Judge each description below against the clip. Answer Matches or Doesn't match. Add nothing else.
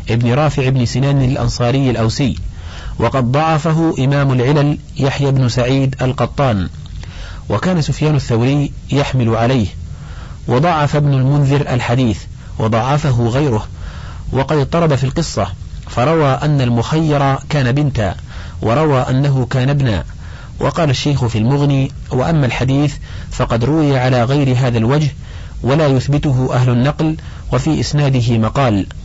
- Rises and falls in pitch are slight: Doesn't match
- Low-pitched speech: Matches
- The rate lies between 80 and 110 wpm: Doesn't match